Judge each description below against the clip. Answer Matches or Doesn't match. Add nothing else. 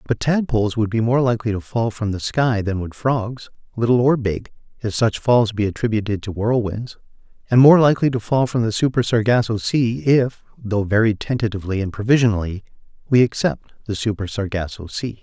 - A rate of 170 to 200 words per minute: Matches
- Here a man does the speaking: Matches